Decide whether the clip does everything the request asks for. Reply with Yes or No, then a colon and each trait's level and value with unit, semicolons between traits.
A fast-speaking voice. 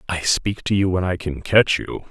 Yes: fast, 255 wpm